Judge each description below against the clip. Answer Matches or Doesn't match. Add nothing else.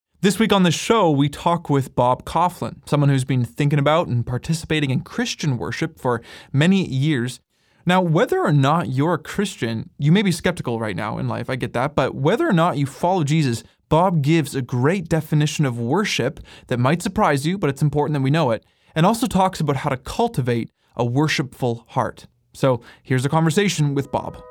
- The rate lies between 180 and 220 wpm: Matches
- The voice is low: Doesn't match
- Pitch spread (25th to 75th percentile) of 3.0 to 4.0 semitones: Doesn't match